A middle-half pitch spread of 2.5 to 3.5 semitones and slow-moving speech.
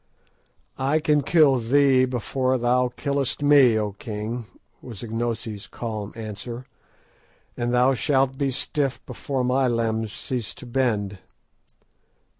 Yes: average, 2.9 semitones; slow, 120 wpm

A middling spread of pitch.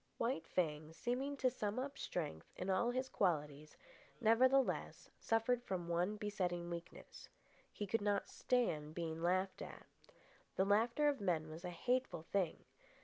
No: wide, 6.1 semitones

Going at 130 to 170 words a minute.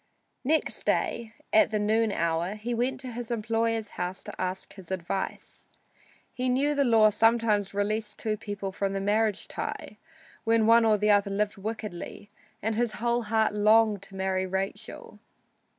Yes: average, 165 wpm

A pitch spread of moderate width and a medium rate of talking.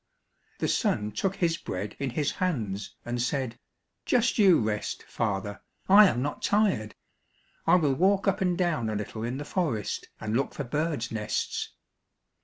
No: wide, 8.8 semitones; average, 165 wpm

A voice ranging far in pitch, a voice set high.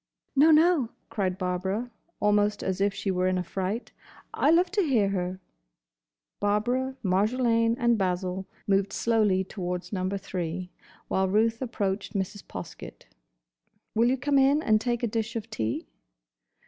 No: average, 4.1 semitones; high, 205 Hz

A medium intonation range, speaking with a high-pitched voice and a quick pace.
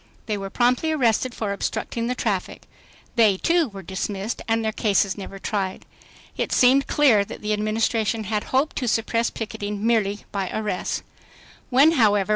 No: average, 3.1 semitones; high, 220 Hz; average, 155 wpm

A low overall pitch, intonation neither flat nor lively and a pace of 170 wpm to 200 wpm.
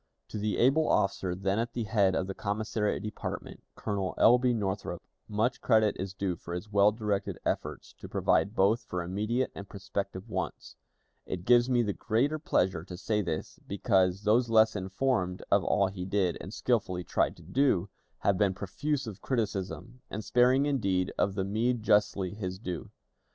Yes: low, 100 Hz; average, 3.5 semitones; average, 175 wpm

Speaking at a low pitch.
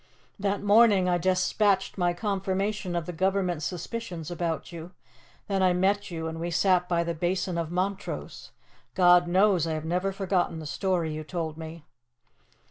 No: medium, 180 Hz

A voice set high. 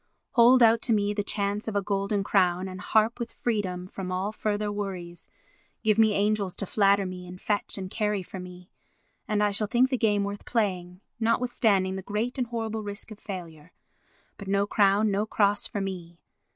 Yes: high, 205 Hz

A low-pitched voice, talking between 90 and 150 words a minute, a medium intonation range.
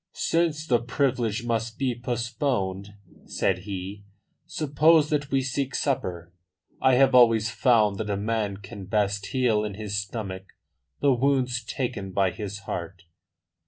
Yes: low, 115 Hz; average, 140 wpm; average, 4.6 semitones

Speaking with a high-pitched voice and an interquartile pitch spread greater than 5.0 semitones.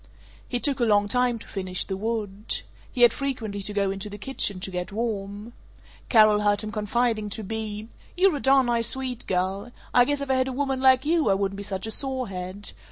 No: high, 220 Hz; average, 4.0 semitones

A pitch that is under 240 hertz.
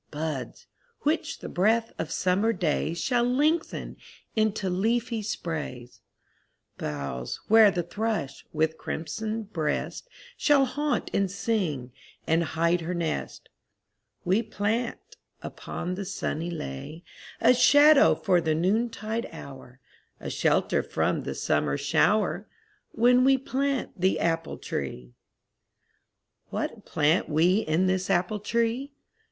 Yes: high, 190 Hz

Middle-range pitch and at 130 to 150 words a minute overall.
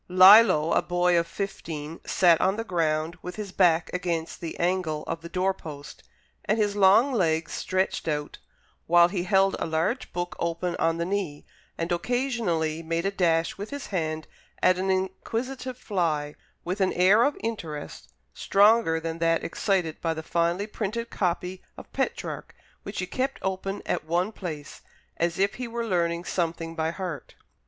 No: medium, 180 Hz; average, 170 wpm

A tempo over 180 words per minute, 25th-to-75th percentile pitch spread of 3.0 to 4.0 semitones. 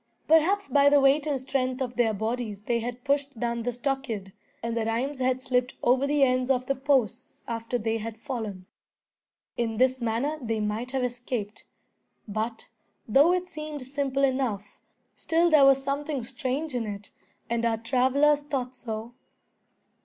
No: average, 165 wpm; average, 3.3 semitones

